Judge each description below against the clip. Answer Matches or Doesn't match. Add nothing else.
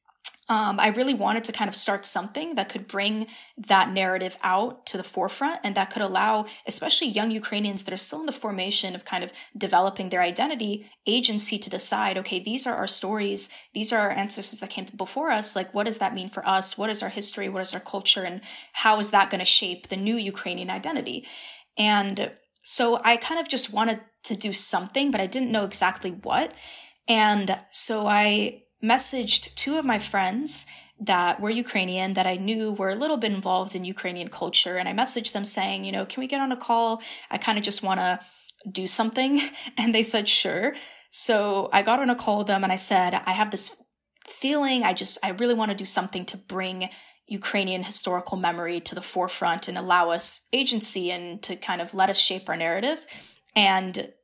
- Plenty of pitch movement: Doesn't match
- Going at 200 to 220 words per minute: Matches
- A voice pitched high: Matches